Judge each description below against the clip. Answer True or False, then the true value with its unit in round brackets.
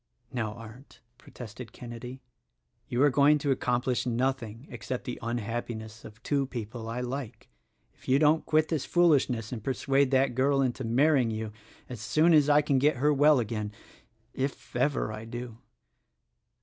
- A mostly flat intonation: False (3.5 semitones)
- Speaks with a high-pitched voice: False (125 Hz)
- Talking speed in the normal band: True (160 wpm)